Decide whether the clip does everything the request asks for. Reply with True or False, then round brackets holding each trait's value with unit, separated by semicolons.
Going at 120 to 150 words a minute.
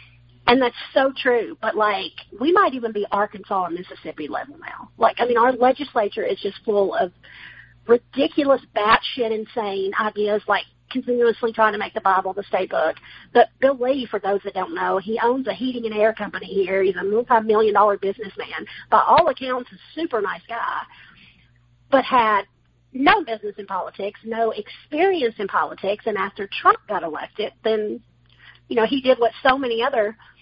False (180 wpm)